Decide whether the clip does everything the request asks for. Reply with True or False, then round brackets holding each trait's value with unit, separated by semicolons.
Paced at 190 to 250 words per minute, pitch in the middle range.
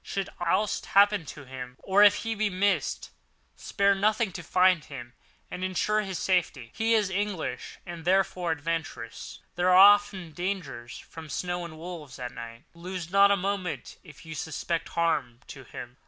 False (170 wpm; 180 Hz)